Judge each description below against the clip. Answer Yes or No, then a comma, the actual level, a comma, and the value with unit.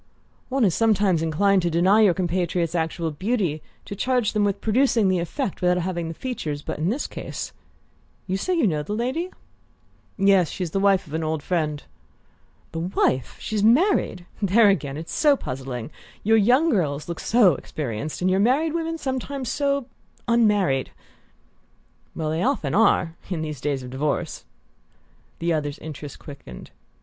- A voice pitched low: No, medium, 185 Hz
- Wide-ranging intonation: Yes, wide, 6.2 semitones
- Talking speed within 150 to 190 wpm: Yes, average, 165 wpm